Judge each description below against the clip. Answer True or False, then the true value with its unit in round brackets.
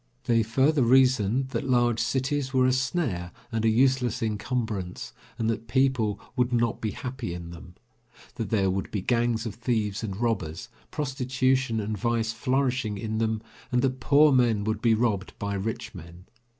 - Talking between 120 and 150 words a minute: False (170 wpm)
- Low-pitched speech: True (115 Hz)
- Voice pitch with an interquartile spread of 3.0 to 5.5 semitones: True (3.4 semitones)